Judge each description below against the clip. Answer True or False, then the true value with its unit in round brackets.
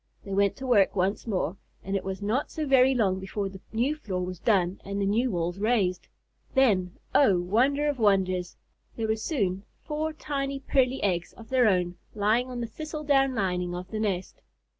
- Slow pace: False (195 wpm)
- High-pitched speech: True (210 Hz)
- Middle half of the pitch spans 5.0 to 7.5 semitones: True (5.6 semitones)